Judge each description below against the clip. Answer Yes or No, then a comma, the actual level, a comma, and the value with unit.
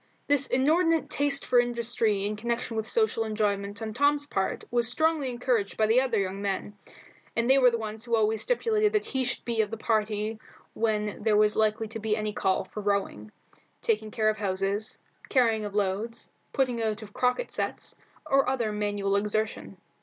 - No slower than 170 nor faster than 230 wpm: Yes, average, 185 wpm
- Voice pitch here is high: Yes, high, 220 Hz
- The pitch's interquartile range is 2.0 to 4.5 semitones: Yes, average, 3.0 semitones